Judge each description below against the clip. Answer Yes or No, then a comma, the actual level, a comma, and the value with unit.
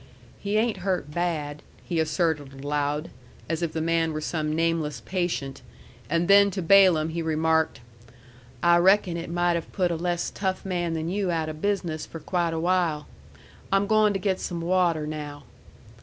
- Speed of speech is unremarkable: Yes, average, 175 wpm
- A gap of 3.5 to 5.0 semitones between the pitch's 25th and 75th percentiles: No, average, 2.7 semitones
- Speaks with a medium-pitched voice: Yes, medium, 170 Hz